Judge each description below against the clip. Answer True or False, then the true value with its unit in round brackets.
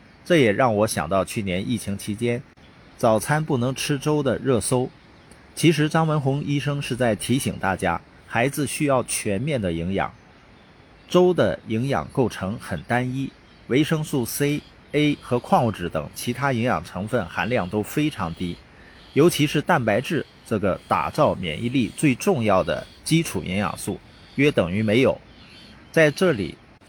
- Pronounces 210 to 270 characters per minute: True (230 characters per minute)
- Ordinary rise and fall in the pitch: False (6.4 semitones)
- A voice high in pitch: False (125 Hz)